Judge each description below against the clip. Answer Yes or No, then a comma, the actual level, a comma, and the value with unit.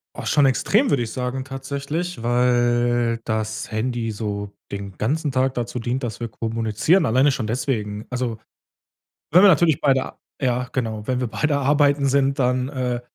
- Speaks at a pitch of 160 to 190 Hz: No, low, 125 Hz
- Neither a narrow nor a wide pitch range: Yes, average, 3.3 semitones